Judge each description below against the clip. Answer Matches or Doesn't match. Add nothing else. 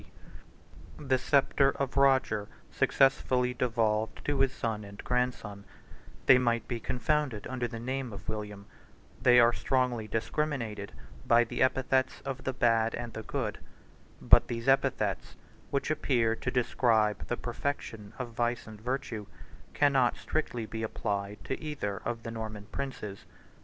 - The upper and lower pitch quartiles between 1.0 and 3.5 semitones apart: Matches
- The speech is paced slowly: Doesn't match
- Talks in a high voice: Doesn't match